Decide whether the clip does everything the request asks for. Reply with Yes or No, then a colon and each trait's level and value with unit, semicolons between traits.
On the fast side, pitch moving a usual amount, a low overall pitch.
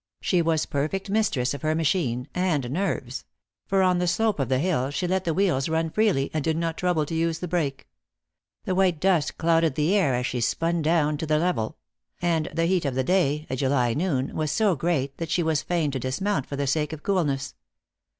No: fast, 220 wpm; average, 4.2 semitones; medium, 160 Hz